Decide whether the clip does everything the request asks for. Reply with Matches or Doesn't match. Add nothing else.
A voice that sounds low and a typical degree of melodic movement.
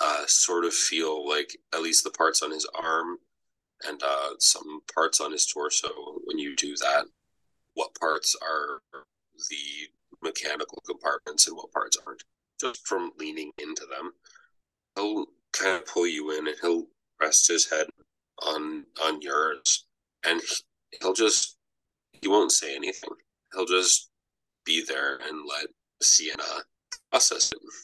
Doesn't match